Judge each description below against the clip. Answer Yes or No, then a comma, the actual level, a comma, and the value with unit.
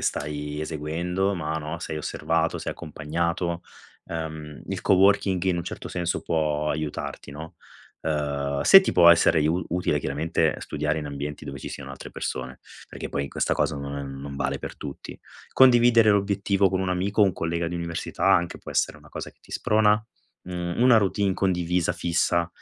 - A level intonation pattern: No, average, 3.8 semitones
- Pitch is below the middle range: Yes, very low, 85 Hz